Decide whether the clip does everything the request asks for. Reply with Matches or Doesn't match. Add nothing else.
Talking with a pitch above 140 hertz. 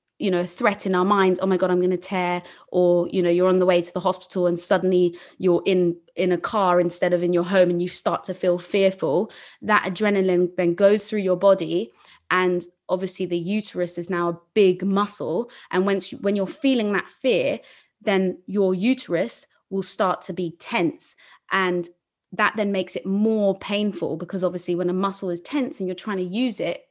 Matches